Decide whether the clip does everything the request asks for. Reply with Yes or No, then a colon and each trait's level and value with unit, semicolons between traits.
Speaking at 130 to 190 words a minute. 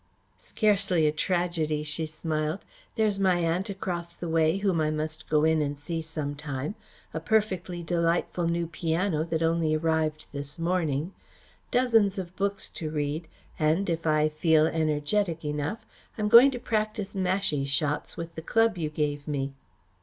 Yes: average, 160 wpm